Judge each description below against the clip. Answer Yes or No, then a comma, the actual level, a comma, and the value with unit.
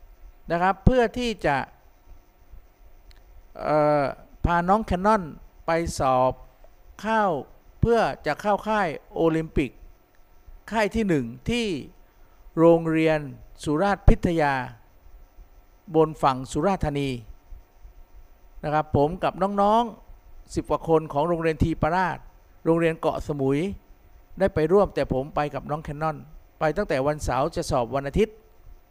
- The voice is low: No, medium, 155 Hz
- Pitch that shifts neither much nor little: No, wide, 5.8 semitones